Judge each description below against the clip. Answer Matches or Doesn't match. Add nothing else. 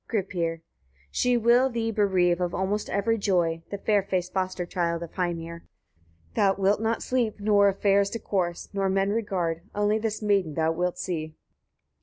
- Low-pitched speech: Doesn't match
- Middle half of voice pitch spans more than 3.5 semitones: Doesn't match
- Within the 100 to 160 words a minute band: Doesn't match